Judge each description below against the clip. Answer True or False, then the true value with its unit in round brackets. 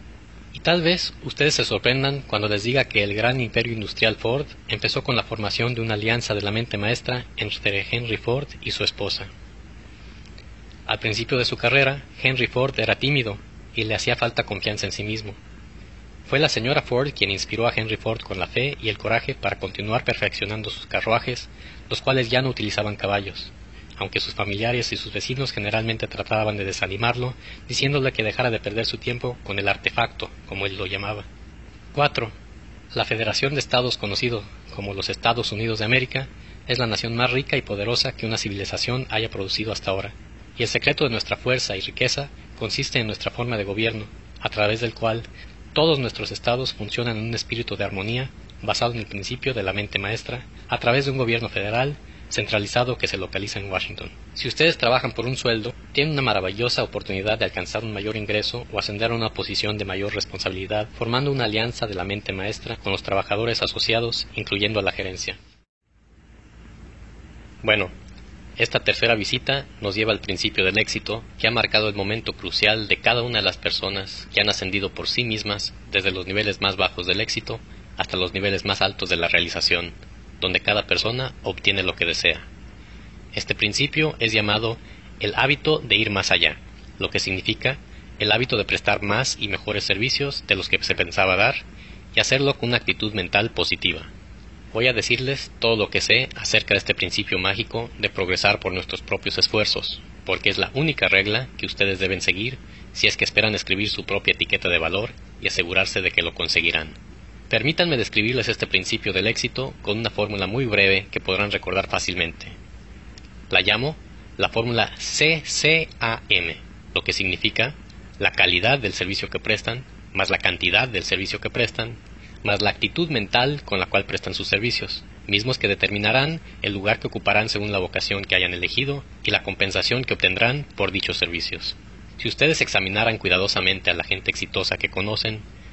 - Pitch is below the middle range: True (105 Hz)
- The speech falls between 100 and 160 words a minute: False (185 wpm)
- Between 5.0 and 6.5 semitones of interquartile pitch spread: False (3.4 semitones)